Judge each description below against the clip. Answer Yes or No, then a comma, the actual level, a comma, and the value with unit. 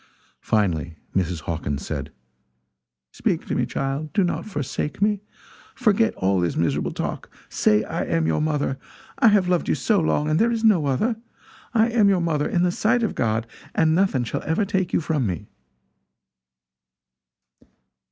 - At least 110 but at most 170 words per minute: Yes, average, 165 wpm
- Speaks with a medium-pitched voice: Yes, medium, 155 Hz